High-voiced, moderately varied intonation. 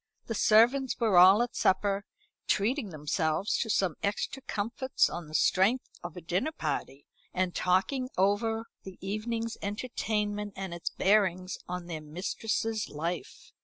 Yes: high, 200 Hz; average, 4.0 semitones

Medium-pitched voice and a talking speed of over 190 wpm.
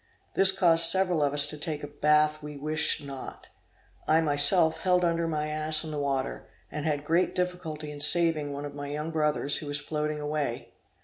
Yes: medium, 150 Hz; average, 200 wpm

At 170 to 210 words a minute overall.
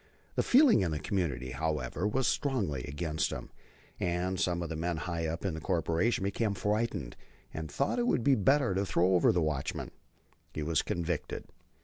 Yes: average, 190 wpm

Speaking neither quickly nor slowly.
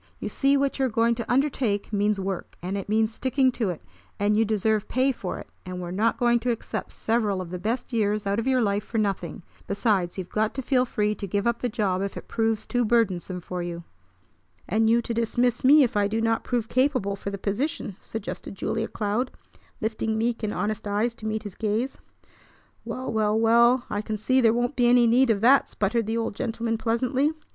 No: fast, 220 wpm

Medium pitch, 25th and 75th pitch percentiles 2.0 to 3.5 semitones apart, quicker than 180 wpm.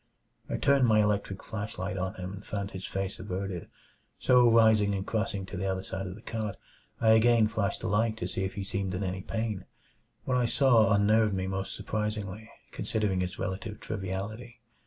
No: low, 105 Hz; narrow, 2.5 semitones; average, 190 wpm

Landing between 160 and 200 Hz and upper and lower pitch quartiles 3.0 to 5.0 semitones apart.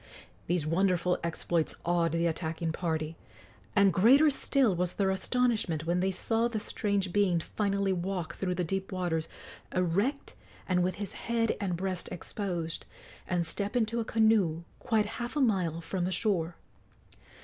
Yes: medium, 185 Hz; average, 3.6 semitones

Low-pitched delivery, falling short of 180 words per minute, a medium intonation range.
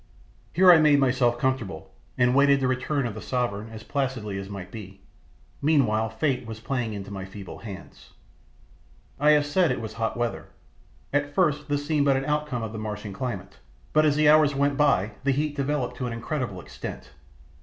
No: low, 125 Hz; average, 190 wpm; average, 4.8 semitones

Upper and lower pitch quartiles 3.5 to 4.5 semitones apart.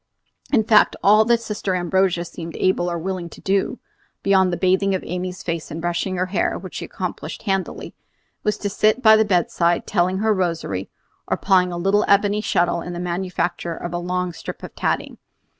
No: narrow, 2.4 semitones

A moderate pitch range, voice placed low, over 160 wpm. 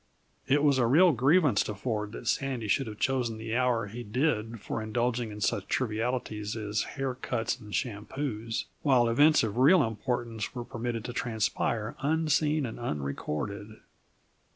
No: average, 3.4 semitones; low, 120 Hz; average, 155 wpm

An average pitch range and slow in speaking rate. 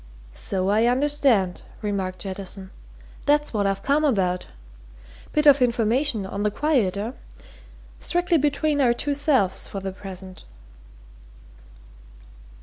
No: wide, 6.9 semitones; slow, 120 wpm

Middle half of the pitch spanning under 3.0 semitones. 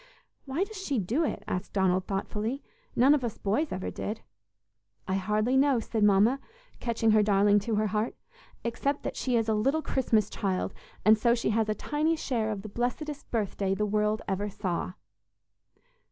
No: average, 4.0 semitones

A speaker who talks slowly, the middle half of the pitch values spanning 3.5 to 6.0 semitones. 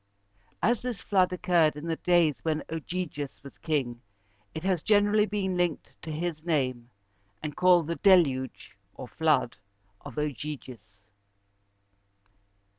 Yes: slow, 130 wpm; average, 4.2 semitones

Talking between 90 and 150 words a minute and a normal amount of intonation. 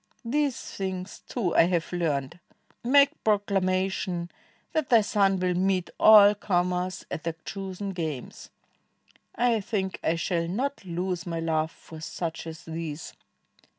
Yes: slow, 135 wpm; average, 3.4 semitones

